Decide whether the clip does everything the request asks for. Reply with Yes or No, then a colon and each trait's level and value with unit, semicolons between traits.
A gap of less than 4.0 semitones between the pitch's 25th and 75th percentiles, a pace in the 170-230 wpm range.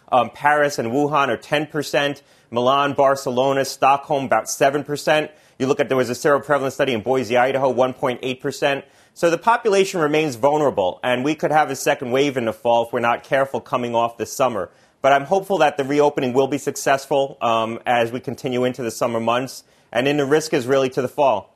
Yes: narrow, 2.6 semitones; average, 200 wpm